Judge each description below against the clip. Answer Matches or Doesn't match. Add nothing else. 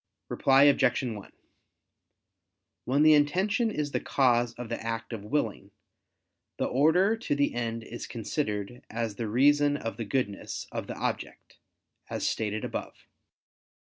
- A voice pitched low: Matches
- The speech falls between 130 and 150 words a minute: Matches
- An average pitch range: Matches